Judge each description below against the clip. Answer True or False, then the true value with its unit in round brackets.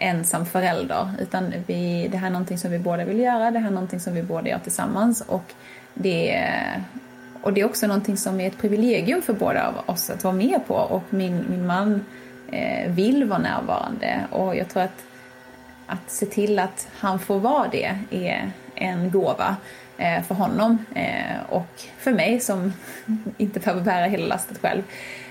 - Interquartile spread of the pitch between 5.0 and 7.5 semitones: False (3.4 semitones)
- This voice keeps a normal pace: True (180 wpm)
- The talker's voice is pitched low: False (195 Hz)